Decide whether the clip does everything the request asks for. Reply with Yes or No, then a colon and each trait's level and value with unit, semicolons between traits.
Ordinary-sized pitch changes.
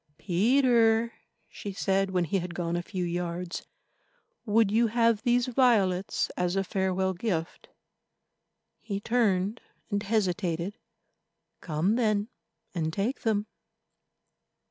Yes: average, 4.0 semitones